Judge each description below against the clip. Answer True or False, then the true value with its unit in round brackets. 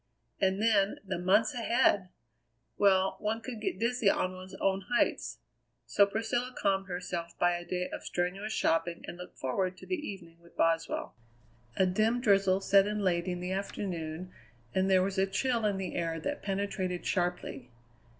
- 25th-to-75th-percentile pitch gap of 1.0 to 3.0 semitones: True (2.6 semitones)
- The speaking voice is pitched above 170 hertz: True (190 Hz)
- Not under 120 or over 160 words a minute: False (170 wpm)